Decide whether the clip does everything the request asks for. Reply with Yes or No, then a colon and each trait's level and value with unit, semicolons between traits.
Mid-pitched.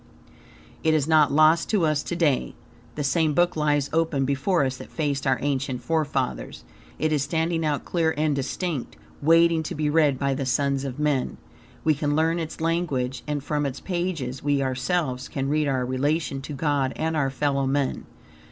Yes: medium, 145 Hz